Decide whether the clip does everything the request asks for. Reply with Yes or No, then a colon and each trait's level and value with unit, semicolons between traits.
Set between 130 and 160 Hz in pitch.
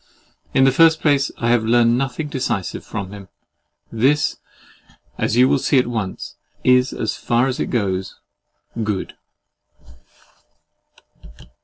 No: low, 120 Hz